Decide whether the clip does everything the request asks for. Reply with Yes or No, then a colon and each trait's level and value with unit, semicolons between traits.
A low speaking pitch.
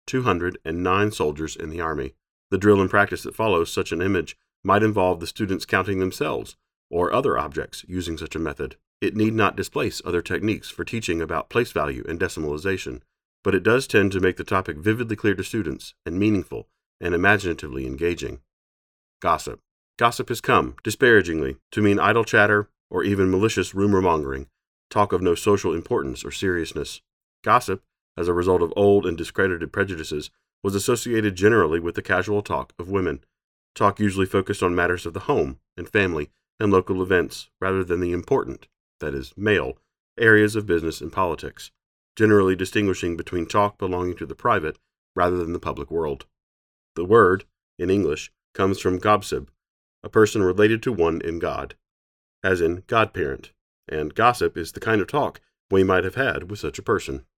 Yes: very low, 95 Hz